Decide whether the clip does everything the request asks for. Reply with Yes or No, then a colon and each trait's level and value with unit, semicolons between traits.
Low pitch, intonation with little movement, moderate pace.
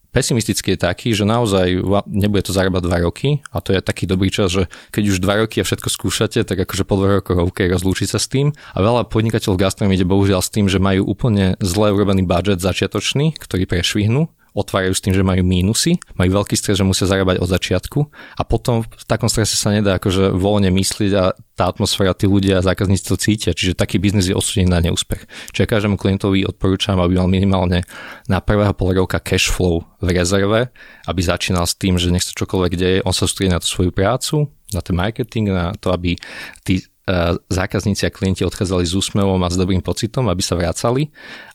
No: very low, 95 Hz; narrow, 2.3 semitones; fast, 205 wpm